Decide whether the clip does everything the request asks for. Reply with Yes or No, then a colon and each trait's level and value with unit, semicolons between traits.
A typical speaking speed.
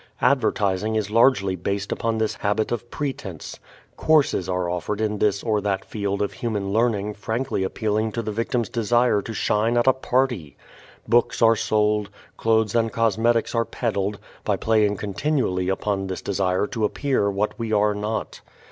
Yes: average, 165 wpm